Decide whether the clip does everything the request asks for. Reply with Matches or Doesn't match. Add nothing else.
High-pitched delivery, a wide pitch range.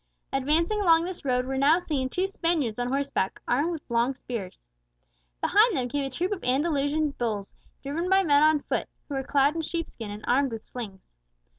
Doesn't match